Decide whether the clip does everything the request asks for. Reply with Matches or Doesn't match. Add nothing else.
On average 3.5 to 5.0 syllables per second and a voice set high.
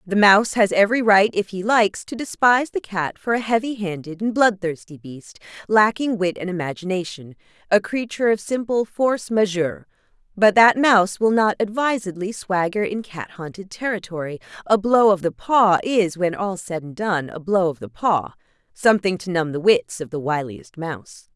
Doesn't match